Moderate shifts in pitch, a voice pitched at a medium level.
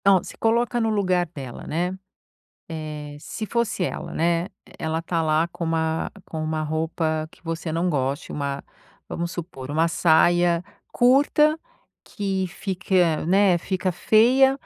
Yes: average, 3.6 semitones; medium, 170 Hz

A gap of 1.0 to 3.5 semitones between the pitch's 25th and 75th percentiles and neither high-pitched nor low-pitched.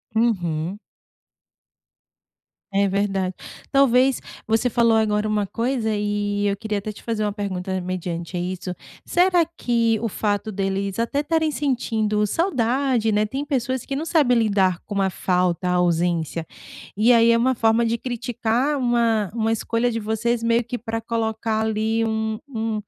No: average, 2.9 semitones; high, 220 Hz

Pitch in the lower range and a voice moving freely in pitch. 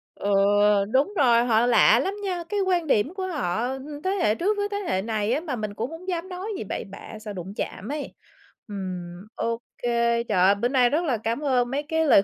No: high, 245 Hz; wide, 7.3 semitones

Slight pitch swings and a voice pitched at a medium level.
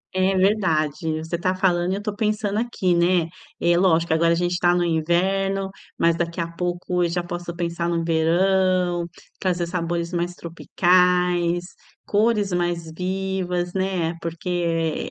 Yes: narrow, 1.8 semitones; medium, 175 Hz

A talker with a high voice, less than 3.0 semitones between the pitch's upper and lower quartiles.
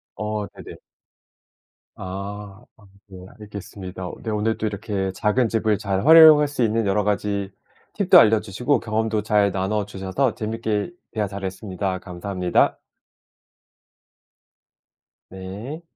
No: low, 105 Hz; narrow, 2.4 semitones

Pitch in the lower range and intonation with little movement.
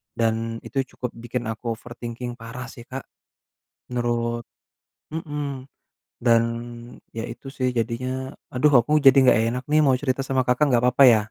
Yes: low, 125 Hz; narrow, 2.3 semitones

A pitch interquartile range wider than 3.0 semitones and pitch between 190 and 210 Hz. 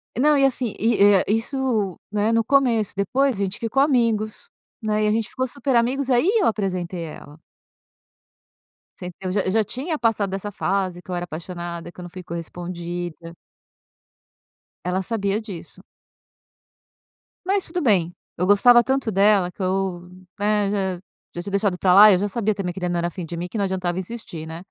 Yes: average, 4.2 semitones; high, 200 Hz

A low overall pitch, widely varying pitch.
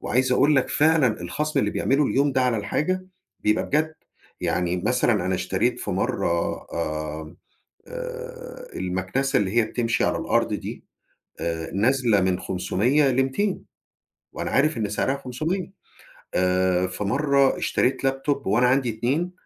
Yes: low, 125 Hz; wide, 7.6 semitones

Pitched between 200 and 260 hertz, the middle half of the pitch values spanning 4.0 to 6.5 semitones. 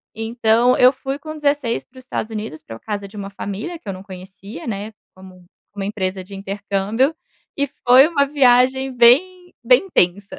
Yes: high, 225 Hz; average, 5.3 semitones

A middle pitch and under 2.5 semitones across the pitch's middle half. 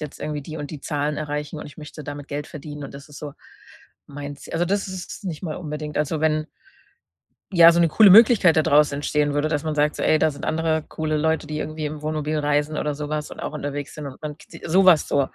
Yes: medium, 150 Hz; narrow, 1.3 semitones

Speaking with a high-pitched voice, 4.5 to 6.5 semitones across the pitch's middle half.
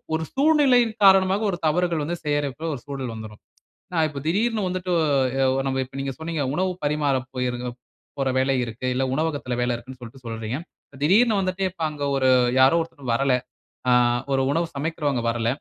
No: medium, 145 Hz; wide, 5.5 semitones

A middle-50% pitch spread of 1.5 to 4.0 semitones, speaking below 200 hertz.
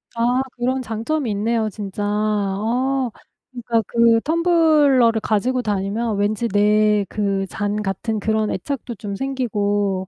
No: average, 3.3 semitones; high, 220 Hz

